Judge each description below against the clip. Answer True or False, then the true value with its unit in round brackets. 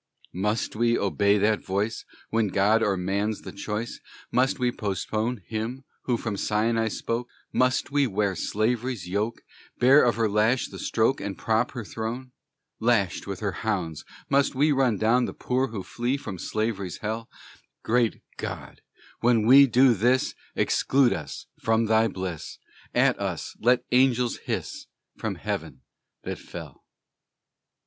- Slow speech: False (150 wpm)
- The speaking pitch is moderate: False (115 Hz)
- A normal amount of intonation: True (3.0 semitones)